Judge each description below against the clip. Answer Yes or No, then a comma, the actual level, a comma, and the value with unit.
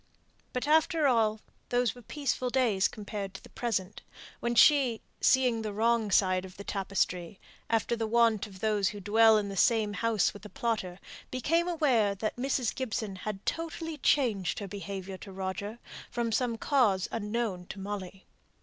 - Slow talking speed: No, average, 165 wpm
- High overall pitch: Yes, high, 220 Hz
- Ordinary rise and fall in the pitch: Yes, average, 3.6 semitones